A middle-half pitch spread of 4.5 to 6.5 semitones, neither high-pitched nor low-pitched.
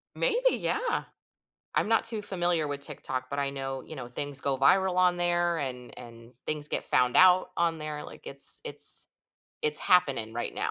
Yes: average, 4.9 semitones; medium, 150 Hz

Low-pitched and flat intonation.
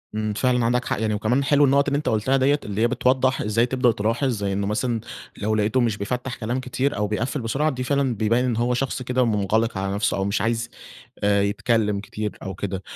No: low, 115 Hz; average, 3.5 semitones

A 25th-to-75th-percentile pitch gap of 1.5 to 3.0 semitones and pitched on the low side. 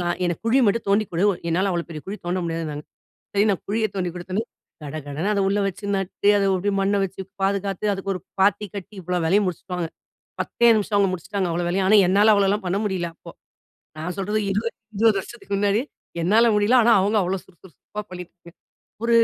No: narrow, 2.6 semitones; high, 195 Hz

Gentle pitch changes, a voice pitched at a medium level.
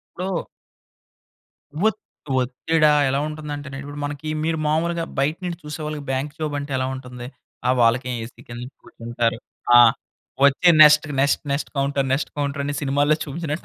Yes: narrow, 2.3 semitones; medium, 145 Hz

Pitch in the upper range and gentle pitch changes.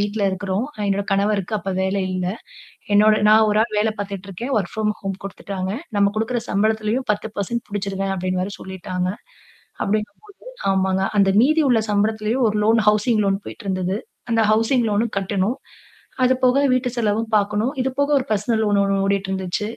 Yes: high, 205 Hz; narrow, 2.2 semitones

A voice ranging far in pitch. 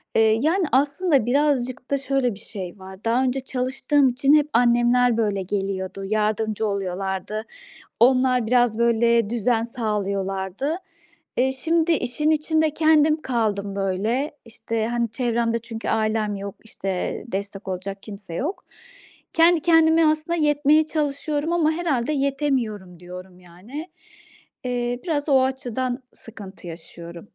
Yes: wide, 5.8 semitones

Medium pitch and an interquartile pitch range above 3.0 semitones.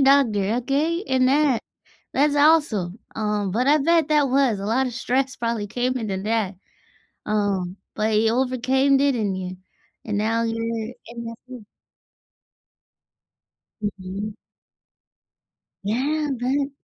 No: high, 235 Hz; average, 4.4 semitones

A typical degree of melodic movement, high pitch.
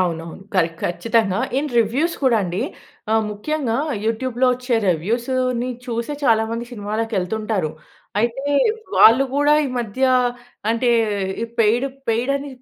Yes: average, 3.3 semitones; high, 230 Hz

